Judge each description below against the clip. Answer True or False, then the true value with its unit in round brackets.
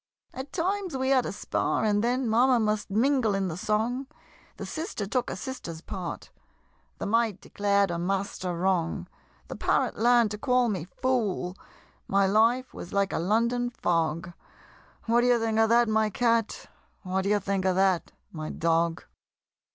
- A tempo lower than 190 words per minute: True (165 wpm)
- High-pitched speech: True (215 Hz)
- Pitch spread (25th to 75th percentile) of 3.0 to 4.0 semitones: False (4.4 semitones)